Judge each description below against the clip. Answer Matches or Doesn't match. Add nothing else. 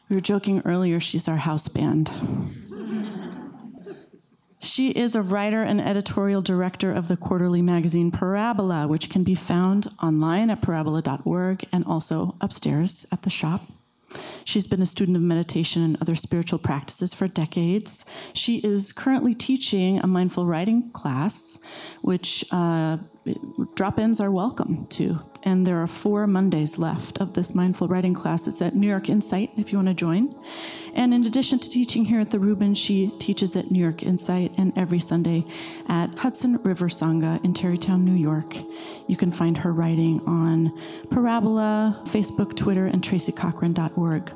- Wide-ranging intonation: Doesn't match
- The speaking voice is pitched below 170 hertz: Doesn't match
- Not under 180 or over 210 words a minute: Doesn't match